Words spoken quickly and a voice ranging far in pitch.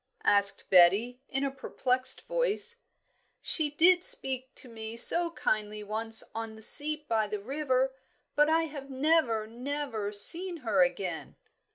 No: average, 145 wpm; wide, 5.7 semitones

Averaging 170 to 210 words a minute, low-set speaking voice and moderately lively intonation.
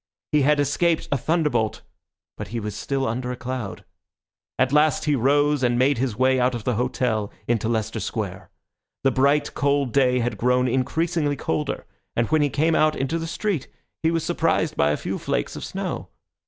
Yes: average, 190 wpm; low, 130 Hz; average, 3.6 semitones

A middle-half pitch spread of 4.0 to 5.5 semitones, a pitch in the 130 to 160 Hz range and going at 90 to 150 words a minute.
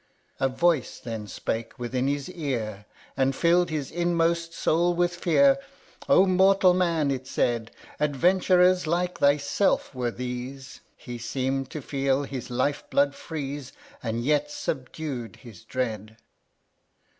Yes: average, 5.2 semitones; medium, 140 Hz; average, 145 wpm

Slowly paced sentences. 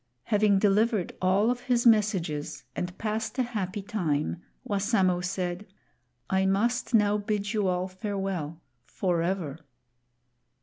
Yes: slow, 120 wpm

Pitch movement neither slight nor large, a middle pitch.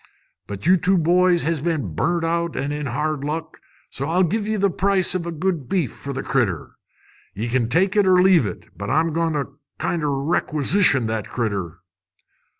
Yes: average, 4.9 semitones; medium, 160 Hz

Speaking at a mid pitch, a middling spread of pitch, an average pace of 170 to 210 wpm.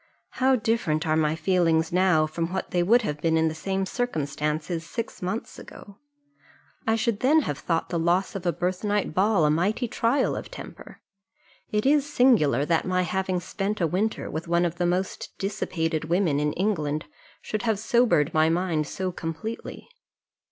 Yes: medium, 180 Hz; average, 4.8 semitones; average, 175 wpm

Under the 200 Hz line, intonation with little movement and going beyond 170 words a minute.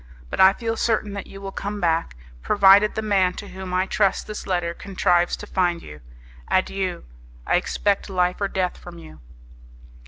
Yes: high, 190 Hz; narrow, 2.2 semitones; average, 180 wpm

